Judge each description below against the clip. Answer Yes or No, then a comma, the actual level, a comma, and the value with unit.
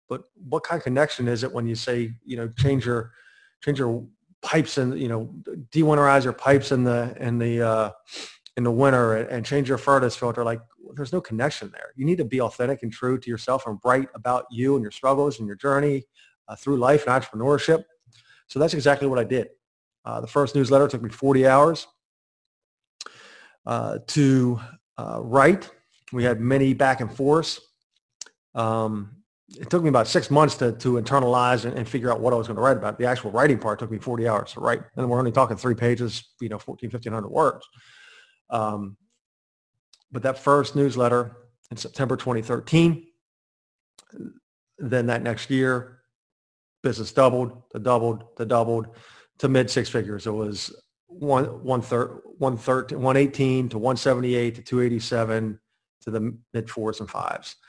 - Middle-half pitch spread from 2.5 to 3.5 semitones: Yes, average, 2.9 semitones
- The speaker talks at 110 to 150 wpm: No, average, 175 wpm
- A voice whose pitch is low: Yes, low, 125 Hz